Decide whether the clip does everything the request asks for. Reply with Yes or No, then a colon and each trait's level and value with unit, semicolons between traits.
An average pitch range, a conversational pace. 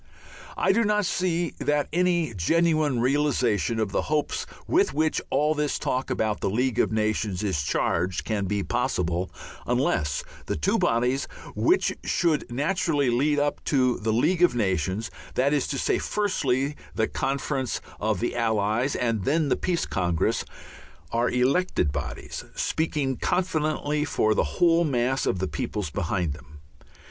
No: wide, 6.3 semitones; average, 155 wpm